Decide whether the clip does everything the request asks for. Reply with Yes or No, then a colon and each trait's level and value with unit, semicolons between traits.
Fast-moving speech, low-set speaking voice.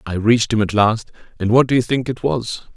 Yes: fast, 260 wpm; low, 115 Hz